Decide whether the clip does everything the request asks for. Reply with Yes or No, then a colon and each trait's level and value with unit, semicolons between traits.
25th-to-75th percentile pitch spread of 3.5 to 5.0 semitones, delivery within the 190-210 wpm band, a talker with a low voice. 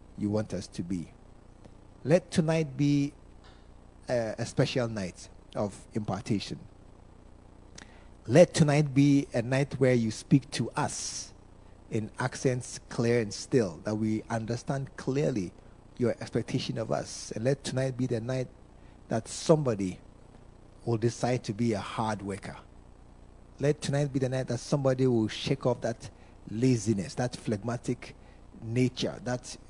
No: average, 4.5 semitones; slow, 135 wpm; low, 115 Hz